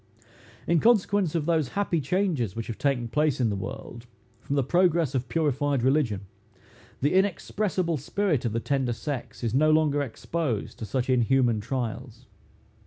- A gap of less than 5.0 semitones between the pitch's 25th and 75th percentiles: No, wide, 5.5 semitones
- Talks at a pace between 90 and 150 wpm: No, average, 160 wpm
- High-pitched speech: No, medium, 140 Hz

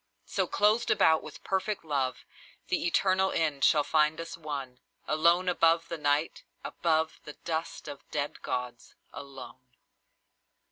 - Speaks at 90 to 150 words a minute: Yes, average, 140 wpm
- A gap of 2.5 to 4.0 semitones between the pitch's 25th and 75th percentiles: Yes, average, 2.8 semitones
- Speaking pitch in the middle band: Yes, medium, 155 Hz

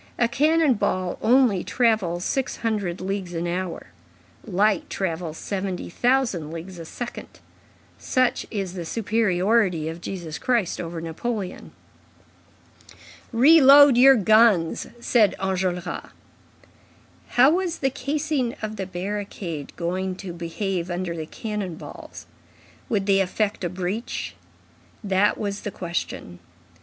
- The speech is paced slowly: Yes, slow, 120 wpm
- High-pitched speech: Yes, high, 195 Hz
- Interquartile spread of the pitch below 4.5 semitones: No, average, 5.0 semitones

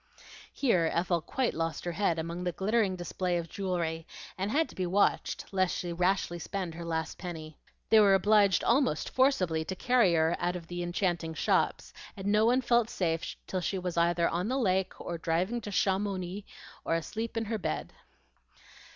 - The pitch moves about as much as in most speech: Yes, average, 3.5 semitones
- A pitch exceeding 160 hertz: Yes, medium, 185 Hz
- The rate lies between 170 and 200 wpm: Yes, average, 185 wpm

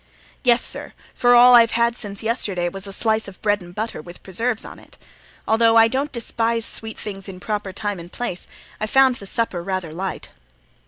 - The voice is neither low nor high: No, high, 220 Hz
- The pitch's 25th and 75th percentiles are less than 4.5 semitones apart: Yes, average, 3.4 semitones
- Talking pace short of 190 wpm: No, average, 200 wpm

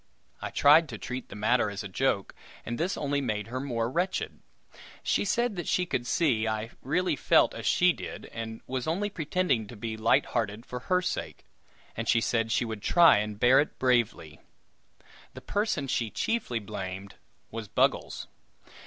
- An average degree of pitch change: No, wide, 6.3 semitones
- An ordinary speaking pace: Yes, average, 180 wpm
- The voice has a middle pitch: No, low, 120 Hz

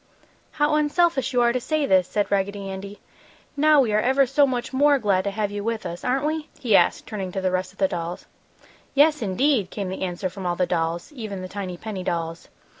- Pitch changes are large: Yes, wide, 6.5 semitones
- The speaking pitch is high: Yes, high, 205 Hz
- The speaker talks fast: Yes, fast, 225 wpm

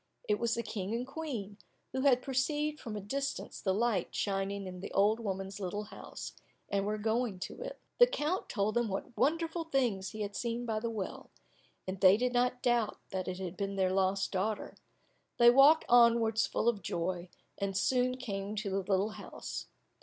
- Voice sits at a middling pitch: No, high, 215 Hz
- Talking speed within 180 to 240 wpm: Yes, average, 190 wpm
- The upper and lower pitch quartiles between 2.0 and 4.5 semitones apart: Yes, average, 4.2 semitones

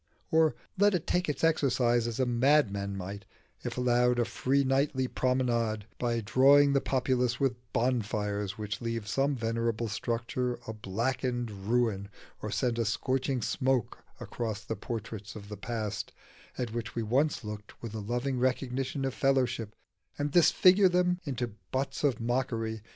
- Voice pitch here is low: Yes, low, 120 Hz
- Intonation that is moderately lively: Yes, average, 3.2 semitones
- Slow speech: No, average, 155 wpm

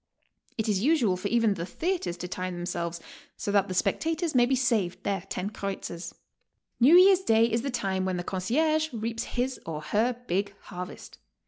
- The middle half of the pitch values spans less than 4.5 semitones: No, wide, 5.4 semitones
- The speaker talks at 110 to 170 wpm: No, average, 185 wpm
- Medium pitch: No, high, 210 Hz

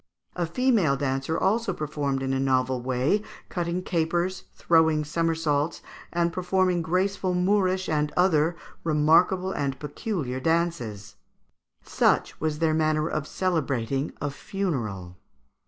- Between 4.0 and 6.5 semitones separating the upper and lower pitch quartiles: Yes, average, 4.4 semitones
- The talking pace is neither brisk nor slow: No, slow, 120 wpm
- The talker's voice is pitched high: No, medium, 160 Hz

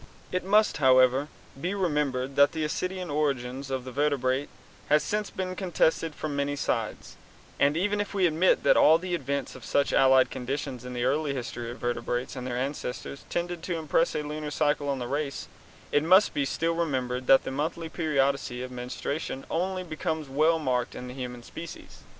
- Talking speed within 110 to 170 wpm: No, average, 185 wpm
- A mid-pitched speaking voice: Yes, medium, 145 Hz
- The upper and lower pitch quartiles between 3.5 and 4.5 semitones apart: Yes, average, 4.2 semitones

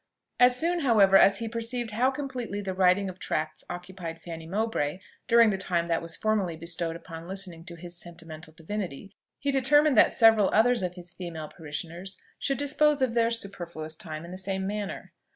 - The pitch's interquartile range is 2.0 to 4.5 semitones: No, average, 5.3 semitones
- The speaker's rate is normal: Yes, average, 185 wpm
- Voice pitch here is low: No, high, 190 Hz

